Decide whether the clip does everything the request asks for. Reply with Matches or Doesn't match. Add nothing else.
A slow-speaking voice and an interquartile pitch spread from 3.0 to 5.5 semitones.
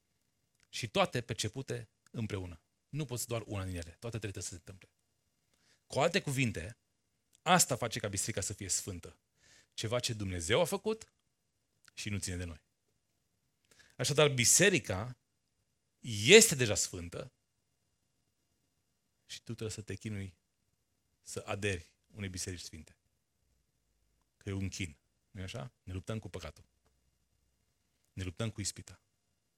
Doesn't match